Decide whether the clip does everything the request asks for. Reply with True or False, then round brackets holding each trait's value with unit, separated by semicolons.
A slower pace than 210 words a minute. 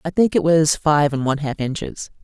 False (240 wpm)